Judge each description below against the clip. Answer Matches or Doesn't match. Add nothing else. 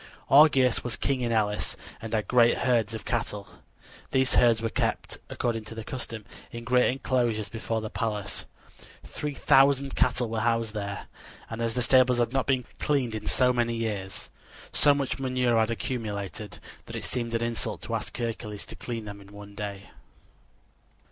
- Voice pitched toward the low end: Matches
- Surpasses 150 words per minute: Matches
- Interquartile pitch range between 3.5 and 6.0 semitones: Doesn't match